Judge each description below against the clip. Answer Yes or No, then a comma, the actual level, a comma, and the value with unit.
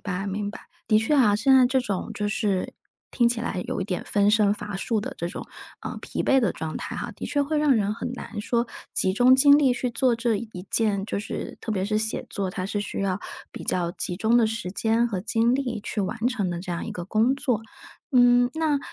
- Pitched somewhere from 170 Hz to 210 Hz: No, high, 220 Hz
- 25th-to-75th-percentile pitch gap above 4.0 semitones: No, average, 3.6 semitones